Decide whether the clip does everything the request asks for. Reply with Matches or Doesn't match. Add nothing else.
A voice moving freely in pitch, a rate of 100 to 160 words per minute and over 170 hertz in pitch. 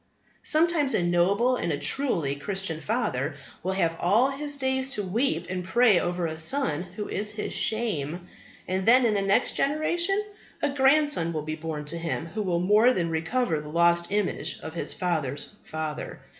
Doesn't match